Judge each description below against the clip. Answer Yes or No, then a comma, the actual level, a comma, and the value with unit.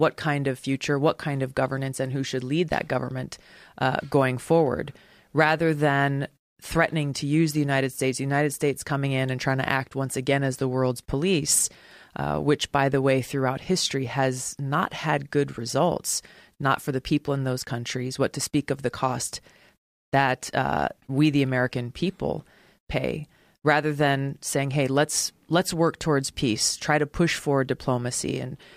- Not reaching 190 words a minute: Yes, average, 180 wpm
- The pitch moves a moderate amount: No, narrow, 2.2 semitones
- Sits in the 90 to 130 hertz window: No, medium, 140 Hz